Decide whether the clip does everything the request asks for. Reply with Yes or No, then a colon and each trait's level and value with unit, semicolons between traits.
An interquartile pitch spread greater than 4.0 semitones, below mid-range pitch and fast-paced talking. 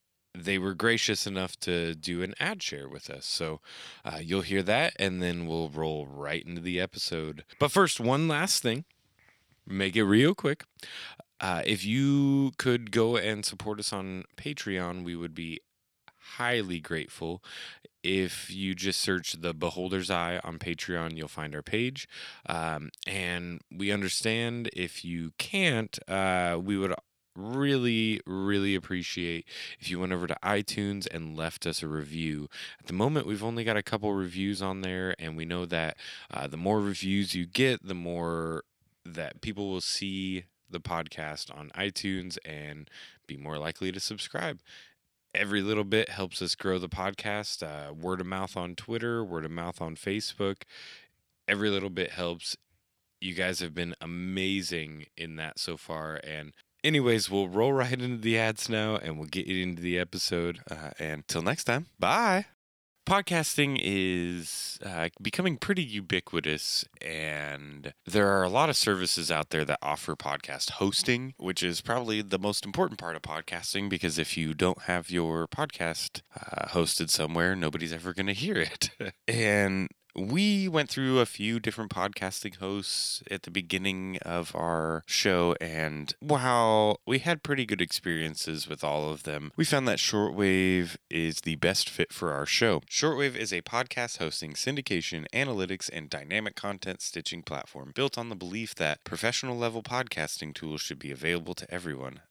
No: average, 4.4 semitones; very low, 95 Hz; average, 165 wpm